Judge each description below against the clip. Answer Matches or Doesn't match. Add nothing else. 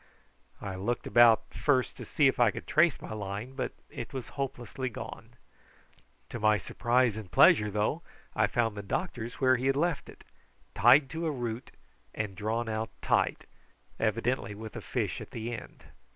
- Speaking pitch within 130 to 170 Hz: Doesn't match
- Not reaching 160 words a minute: Doesn't match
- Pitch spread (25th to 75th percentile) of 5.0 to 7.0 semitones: Doesn't match